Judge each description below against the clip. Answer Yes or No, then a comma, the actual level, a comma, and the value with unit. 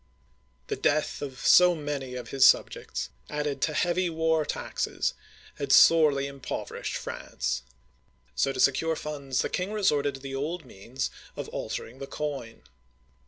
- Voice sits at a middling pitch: Yes, medium, 145 Hz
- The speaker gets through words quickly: No, average, 145 wpm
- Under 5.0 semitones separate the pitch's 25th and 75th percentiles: Yes, average, 3.1 semitones